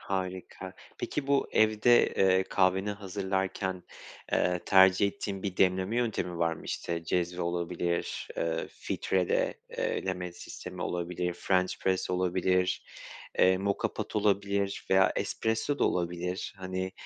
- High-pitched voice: No, very low, 95 Hz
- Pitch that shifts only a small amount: Yes, narrow, 1.7 semitones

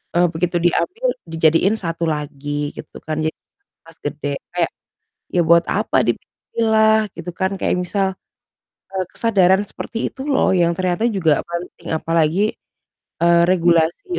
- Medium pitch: Yes, medium, 175 Hz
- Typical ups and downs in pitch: Yes, average, 3.4 semitones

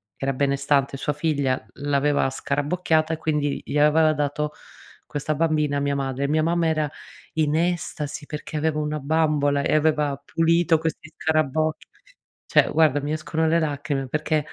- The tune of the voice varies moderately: No, narrow, 1.8 semitones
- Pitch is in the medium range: Yes, medium, 150 Hz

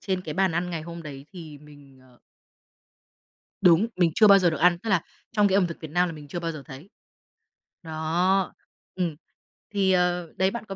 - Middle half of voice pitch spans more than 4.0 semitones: No, average, 3.2 semitones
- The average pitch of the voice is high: No, medium, 175 Hz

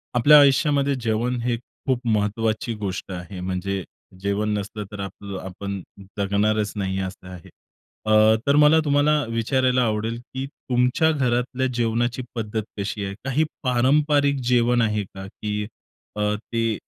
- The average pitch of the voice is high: No, low, 115 Hz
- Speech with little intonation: No, average, 4.2 semitones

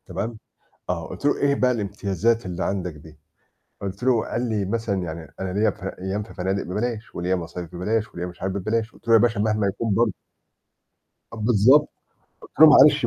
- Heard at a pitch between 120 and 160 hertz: No, low, 100 Hz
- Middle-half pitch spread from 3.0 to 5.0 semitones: Yes, average, 3.6 semitones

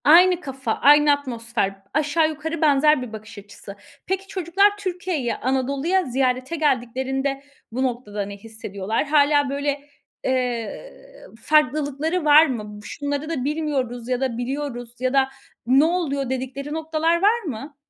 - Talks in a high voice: Yes, very high, 280 Hz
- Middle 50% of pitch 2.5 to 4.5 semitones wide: Yes, average, 3.9 semitones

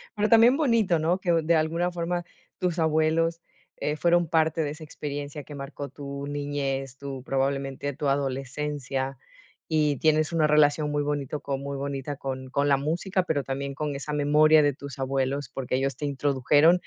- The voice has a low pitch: No, medium, 145 Hz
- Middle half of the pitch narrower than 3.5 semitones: Yes, narrow, 2.5 semitones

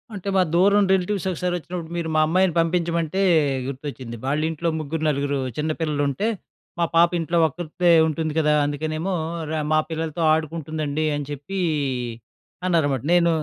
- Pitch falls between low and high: Yes, medium, 160 Hz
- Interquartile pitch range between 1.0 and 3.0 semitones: Yes, narrow, 2.5 semitones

